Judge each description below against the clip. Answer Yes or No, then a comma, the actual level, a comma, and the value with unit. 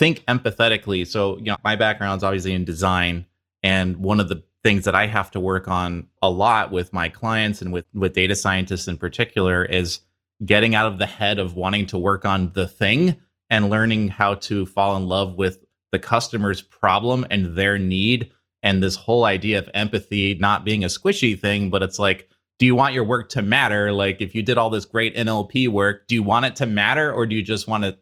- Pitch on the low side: Yes, low, 100 Hz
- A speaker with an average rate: No, fast, 220 wpm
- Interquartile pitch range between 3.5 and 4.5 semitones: No, average, 2.7 semitones